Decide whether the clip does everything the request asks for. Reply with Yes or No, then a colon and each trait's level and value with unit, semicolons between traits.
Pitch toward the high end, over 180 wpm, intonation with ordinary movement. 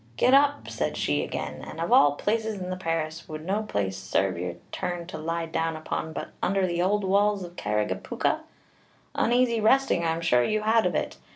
No: medium, 170 Hz; average, 200 wpm; average, 5.0 semitones